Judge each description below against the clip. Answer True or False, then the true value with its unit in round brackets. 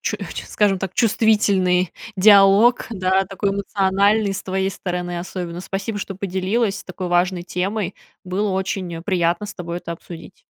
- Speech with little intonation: True (1.9 semitones)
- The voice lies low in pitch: False (190 Hz)